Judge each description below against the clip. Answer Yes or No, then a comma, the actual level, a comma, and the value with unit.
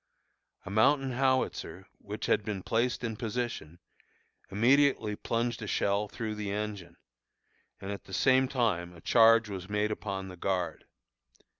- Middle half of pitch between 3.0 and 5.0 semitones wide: Yes, average, 3.5 semitones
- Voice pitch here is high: No, low, 105 Hz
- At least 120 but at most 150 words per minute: Yes, average, 145 wpm